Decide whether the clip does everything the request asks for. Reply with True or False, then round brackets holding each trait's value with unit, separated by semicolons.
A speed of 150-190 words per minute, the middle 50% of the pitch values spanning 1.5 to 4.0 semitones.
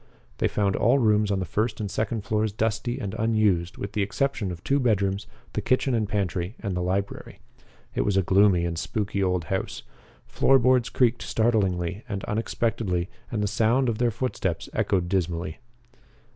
True (175 wpm; 3.2 semitones)